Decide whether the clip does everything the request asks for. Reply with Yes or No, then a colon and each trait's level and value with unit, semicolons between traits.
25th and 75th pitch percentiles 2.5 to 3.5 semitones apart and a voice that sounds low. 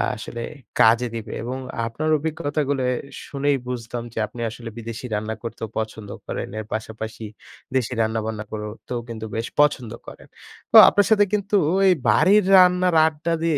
No: wide, 5.5 semitones; low, 120 Hz